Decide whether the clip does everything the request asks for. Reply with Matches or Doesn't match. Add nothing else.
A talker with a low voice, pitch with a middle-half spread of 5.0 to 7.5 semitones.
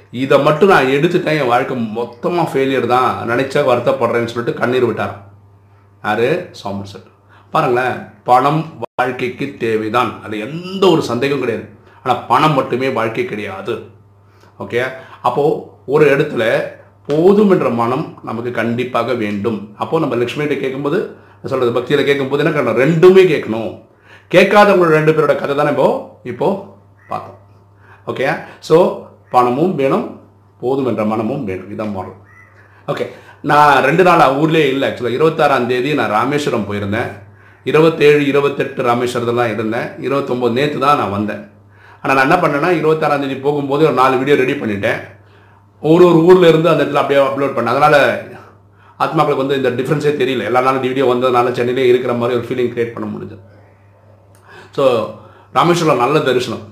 Matches